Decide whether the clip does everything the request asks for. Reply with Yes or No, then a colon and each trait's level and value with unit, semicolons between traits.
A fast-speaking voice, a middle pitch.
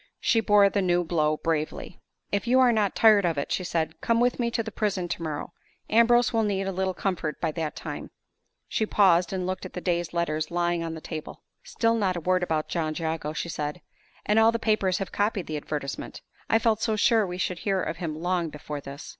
Yes: fast, 225 wpm; medium, 180 Hz